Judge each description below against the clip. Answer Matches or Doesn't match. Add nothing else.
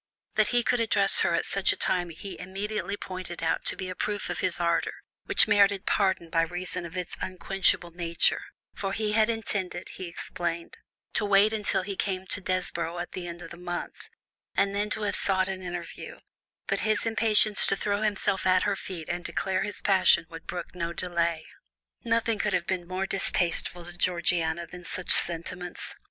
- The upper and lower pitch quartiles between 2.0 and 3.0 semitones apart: Matches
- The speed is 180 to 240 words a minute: Matches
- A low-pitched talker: Doesn't match